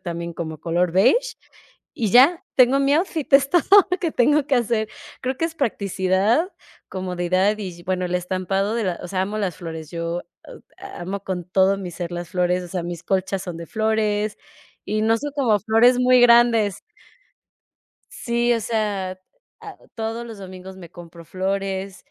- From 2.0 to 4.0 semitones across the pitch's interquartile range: No, average, 4.8 semitones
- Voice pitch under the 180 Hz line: No, high, 195 Hz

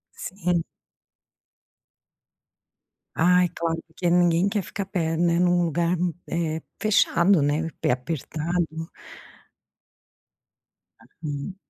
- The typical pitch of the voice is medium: Yes, medium, 170 Hz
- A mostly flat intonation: Yes, narrow, 1.7 semitones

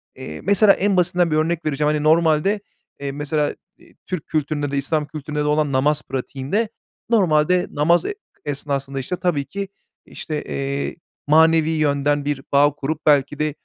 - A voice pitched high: No, medium, 150 Hz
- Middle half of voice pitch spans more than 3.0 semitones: No, narrow, 2.5 semitones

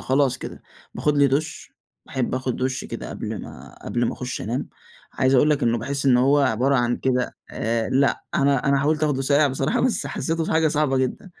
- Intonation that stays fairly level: Yes, narrow, 2.2 semitones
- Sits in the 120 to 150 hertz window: Yes, low, 135 Hz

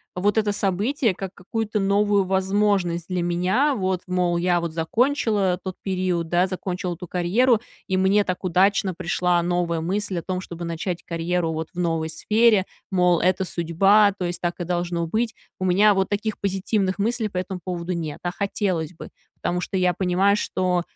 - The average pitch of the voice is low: No, medium, 185 Hz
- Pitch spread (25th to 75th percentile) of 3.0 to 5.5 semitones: No, narrow, 2.4 semitones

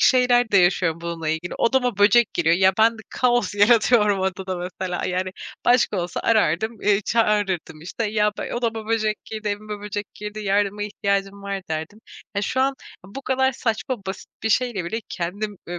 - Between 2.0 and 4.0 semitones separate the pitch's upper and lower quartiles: Yes, average, 3.2 semitones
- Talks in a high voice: Yes, high, 205 Hz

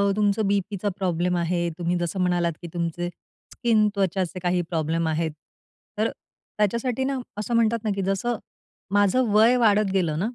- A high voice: Yes, high, 195 Hz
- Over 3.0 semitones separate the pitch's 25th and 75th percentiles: Yes, average, 3.6 semitones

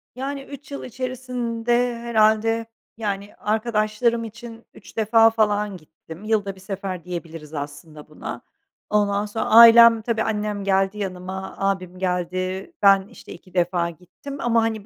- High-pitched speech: Yes, high, 210 Hz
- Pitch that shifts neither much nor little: Yes, average, 3.6 semitones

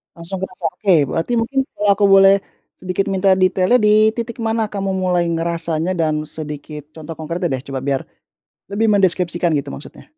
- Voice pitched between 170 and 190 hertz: Yes, medium, 185 Hz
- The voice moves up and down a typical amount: Yes, average, 3.7 semitones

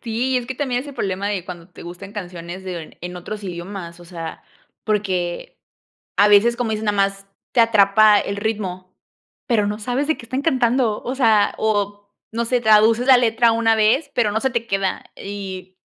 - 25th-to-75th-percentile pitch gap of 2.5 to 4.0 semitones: Yes, average, 3.6 semitones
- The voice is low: No, high, 210 Hz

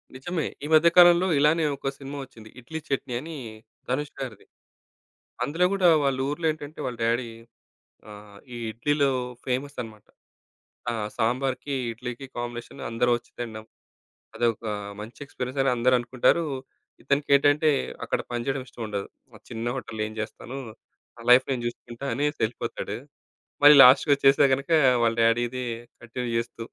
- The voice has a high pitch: No, low, 130 Hz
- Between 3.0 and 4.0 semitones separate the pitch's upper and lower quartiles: Yes, average, 3.3 semitones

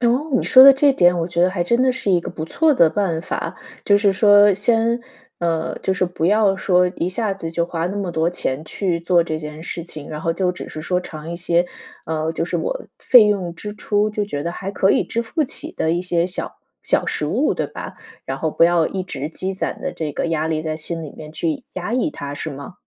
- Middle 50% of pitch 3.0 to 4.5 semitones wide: Yes, average, 4.0 semitones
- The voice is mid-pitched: Yes, medium, 180 Hz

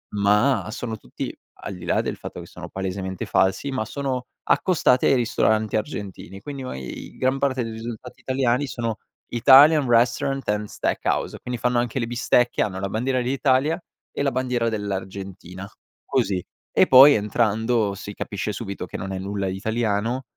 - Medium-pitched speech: No, low, 115 Hz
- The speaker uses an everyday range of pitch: Yes, average, 4.3 semitones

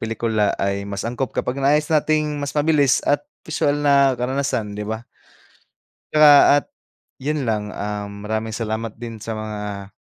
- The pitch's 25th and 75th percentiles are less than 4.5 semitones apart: No, average, 5.3 semitones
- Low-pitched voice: Yes, low, 115 Hz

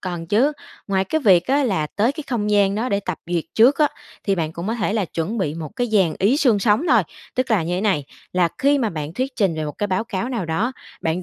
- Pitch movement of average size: No, wide, 5.7 semitones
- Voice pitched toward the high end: Yes, high, 200 Hz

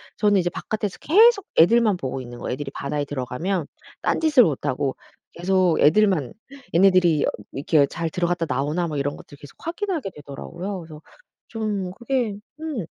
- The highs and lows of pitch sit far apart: Yes, wide, 6.4 semitones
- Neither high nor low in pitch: Yes, medium, 175 Hz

